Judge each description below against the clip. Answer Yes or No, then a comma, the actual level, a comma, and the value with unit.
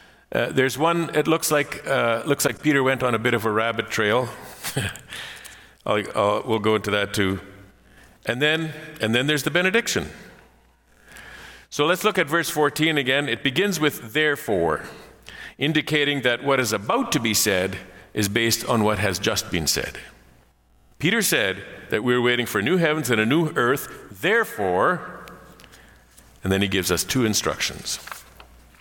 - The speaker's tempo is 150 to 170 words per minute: Yes, average, 165 wpm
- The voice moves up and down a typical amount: No, wide, 6.8 semitones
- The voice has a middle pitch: No, low, 120 Hz